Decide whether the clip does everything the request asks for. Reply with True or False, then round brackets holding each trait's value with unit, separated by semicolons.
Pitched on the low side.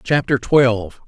True (130 Hz)